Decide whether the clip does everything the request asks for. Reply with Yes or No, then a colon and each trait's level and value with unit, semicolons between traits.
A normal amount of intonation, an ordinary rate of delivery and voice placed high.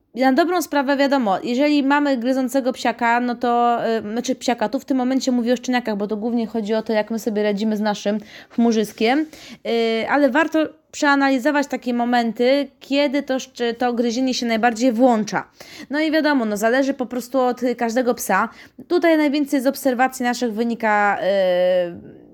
No: average, 3.2 semitones; fast, 170 wpm; very high, 250 Hz